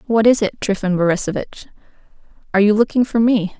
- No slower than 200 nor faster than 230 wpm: No, average, 165 wpm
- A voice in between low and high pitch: No, high, 210 Hz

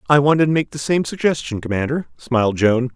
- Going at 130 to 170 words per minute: No, fast, 205 wpm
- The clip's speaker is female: No, male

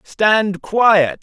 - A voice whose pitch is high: Yes, high, 205 Hz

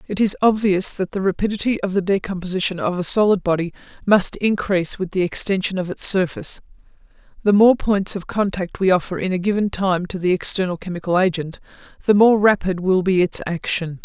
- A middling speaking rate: Yes, average, 190 wpm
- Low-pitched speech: No, high, 190 Hz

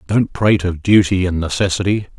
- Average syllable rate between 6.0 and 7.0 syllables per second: No, 5.6 syllables/s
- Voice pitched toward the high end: No, very low, 95 Hz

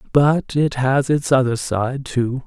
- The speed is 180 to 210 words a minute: No, average, 170 wpm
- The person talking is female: No, male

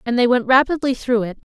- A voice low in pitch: No, high, 240 Hz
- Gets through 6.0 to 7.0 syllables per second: Yes, 6.2 syllables/s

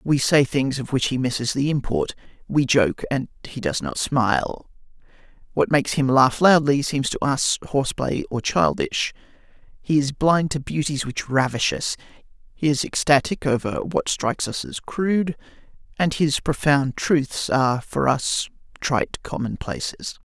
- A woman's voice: No, male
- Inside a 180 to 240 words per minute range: No, average, 155 wpm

